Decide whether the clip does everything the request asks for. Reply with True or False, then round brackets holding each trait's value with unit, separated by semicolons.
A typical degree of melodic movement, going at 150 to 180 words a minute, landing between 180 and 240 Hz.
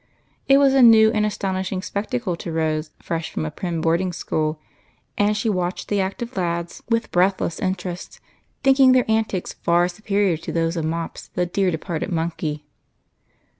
True (4.1 semitones; 165 wpm; 185 Hz)